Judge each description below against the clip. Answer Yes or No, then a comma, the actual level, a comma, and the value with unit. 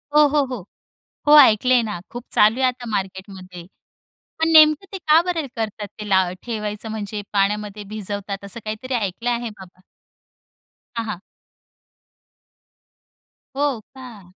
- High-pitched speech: Yes, high, 215 Hz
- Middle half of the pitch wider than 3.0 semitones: Yes, average, 4.1 semitones